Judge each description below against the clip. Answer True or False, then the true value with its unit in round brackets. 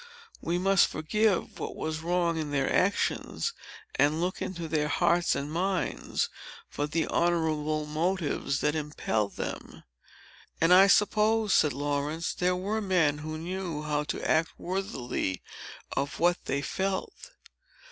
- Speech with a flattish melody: False (3.7 semitones)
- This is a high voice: False (165 Hz)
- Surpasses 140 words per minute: False (135 wpm)